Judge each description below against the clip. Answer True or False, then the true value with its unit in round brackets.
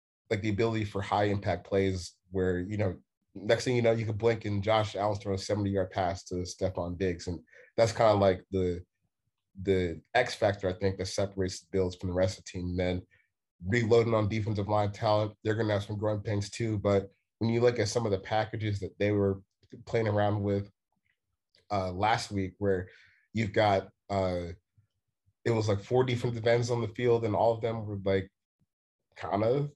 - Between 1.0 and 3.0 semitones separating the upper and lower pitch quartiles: True (2.7 semitones)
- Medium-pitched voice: False (100 Hz)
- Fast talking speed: True (210 wpm)